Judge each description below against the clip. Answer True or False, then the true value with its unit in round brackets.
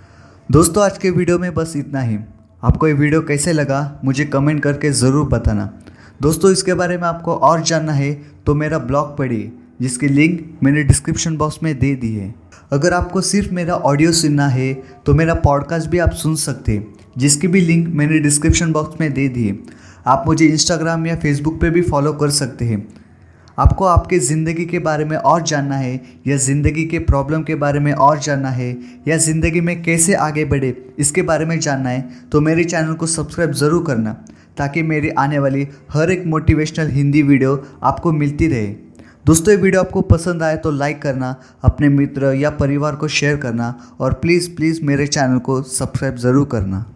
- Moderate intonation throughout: True (3.5 semitones)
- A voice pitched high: False (145 Hz)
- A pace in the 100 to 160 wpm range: False (190 wpm)